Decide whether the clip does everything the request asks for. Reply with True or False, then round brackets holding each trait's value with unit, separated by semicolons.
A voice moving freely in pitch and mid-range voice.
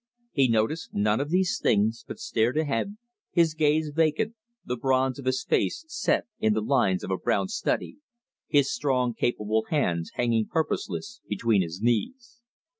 False (6.5 semitones; 130 Hz)